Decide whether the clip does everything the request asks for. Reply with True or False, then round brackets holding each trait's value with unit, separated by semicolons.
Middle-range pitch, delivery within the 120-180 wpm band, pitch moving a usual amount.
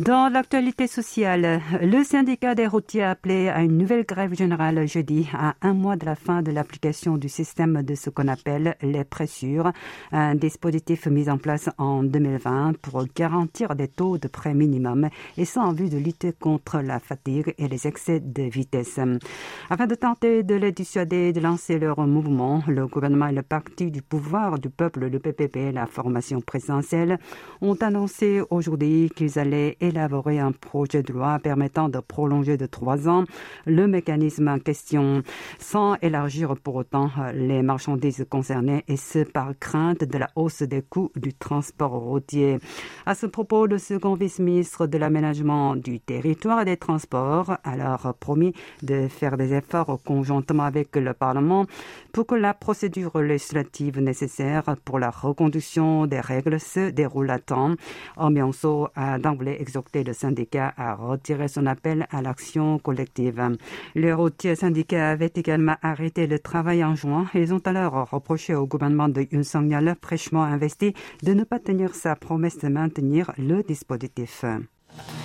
True (155 Hz; 165 wpm; 3.7 semitones)